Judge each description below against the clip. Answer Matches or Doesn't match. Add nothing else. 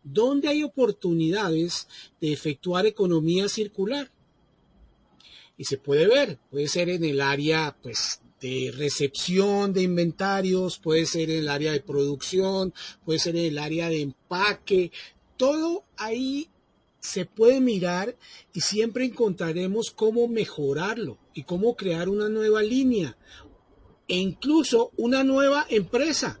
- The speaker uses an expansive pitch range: Matches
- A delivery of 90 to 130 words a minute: Matches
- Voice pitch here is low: Doesn't match